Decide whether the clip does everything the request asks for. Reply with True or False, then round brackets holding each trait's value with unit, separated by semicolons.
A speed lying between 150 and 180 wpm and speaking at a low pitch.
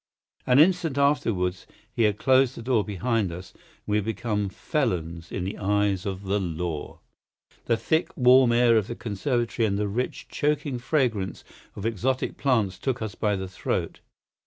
True (170 wpm; 110 Hz)